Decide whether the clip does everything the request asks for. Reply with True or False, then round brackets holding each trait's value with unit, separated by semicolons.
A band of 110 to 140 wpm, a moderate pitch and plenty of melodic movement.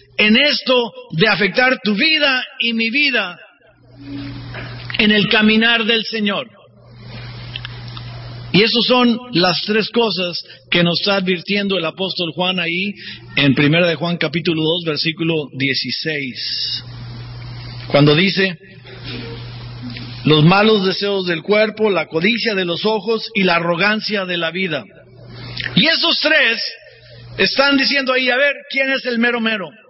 True (135 wpm; 180 Hz; 8.9 semitones)